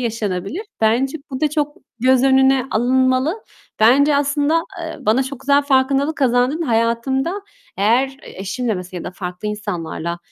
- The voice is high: Yes, very high, 260 Hz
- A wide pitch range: No, average, 4.2 semitones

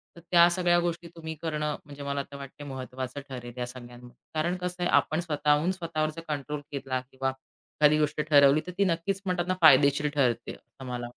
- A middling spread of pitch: Yes, average, 4.1 semitones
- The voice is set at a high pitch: No, medium, 150 Hz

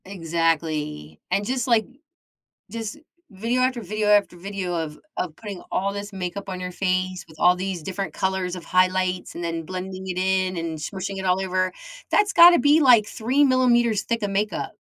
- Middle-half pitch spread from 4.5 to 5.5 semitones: No, average, 3.0 semitones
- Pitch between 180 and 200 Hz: Yes, high, 190 Hz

